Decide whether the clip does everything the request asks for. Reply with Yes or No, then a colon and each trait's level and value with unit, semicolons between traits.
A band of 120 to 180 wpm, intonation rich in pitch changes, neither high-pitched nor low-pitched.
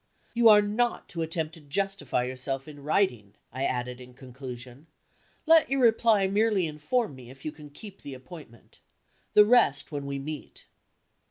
Yes: average, 165 wpm; wide, 7.7 semitones; medium, 150 Hz